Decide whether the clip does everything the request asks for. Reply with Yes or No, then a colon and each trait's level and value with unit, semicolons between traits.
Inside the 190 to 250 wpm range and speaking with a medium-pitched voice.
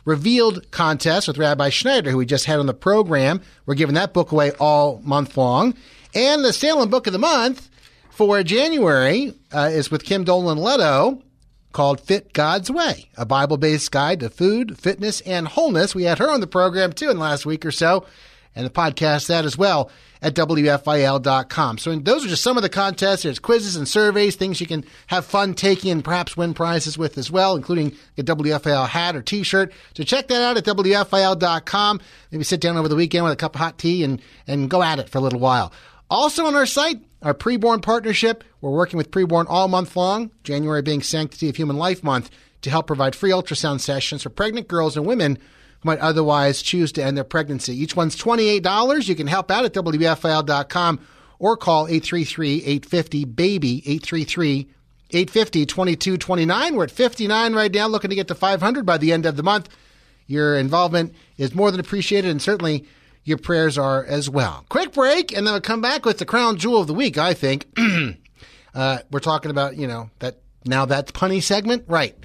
Yes: average, 200 wpm; medium, 165 Hz